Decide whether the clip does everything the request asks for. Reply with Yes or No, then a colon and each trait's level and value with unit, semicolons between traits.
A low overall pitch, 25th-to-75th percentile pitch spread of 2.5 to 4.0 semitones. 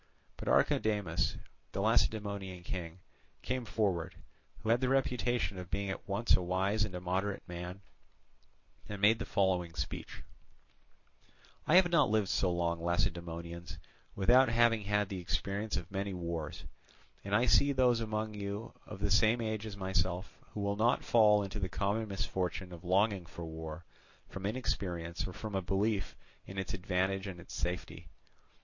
Yes: low, 100 Hz; average, 3.3 semitones